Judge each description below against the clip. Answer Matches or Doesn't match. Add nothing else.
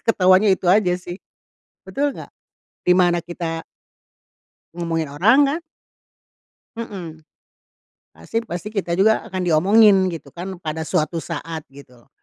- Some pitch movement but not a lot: Matches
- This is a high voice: Doesn't match